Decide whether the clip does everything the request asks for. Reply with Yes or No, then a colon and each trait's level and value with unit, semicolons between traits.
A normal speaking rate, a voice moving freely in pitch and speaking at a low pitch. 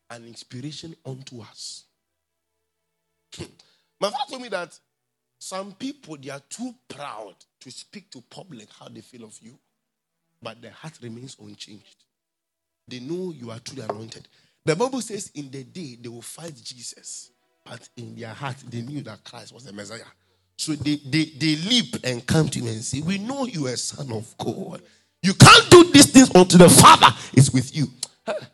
Yes: average, 180 wpm; wide, 6.8 semitones; low, 130 Hz